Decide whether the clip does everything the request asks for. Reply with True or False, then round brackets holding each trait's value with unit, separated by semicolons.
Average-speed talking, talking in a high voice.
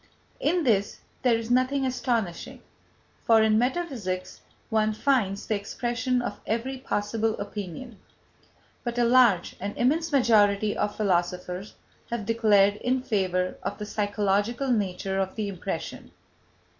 False (130 wpm; 220 Hz)